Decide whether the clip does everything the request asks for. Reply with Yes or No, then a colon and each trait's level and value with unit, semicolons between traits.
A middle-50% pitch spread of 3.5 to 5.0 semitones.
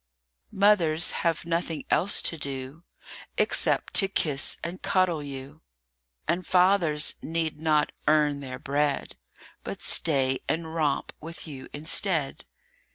No: average, 2.8 semitones